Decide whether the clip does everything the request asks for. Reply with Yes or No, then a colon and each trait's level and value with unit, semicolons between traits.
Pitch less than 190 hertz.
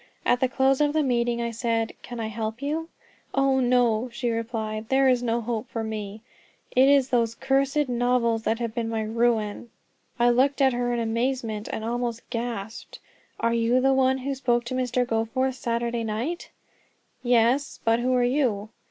No: high, 240 Hz